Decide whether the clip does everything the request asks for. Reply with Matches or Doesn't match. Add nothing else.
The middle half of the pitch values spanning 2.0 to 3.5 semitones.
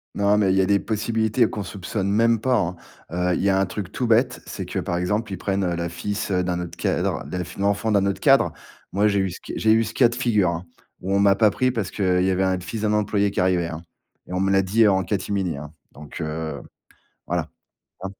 Matches